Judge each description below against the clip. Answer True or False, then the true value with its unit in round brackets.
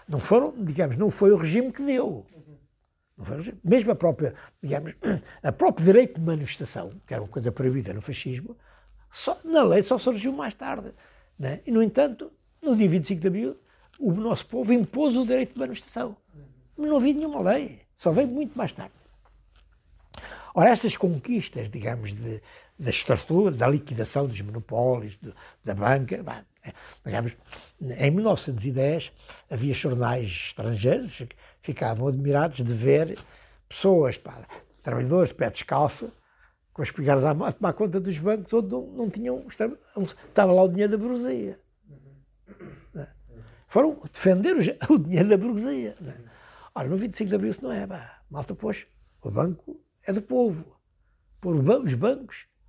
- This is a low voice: False (175 Hz)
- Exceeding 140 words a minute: True (155 wpm)